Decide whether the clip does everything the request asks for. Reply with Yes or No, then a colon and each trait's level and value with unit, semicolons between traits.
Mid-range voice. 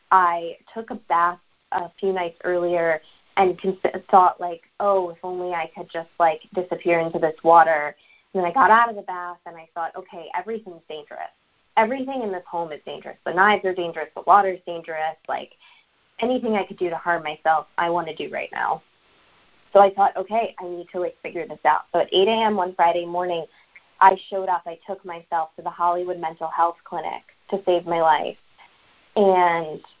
Yes: medium, 175 Hz